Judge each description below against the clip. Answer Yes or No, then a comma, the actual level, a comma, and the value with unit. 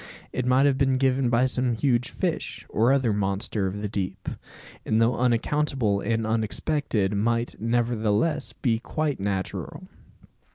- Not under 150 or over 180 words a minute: No, average, 140 wpm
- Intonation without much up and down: No, average, 3.7 semitones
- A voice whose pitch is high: No, low, 115 Hz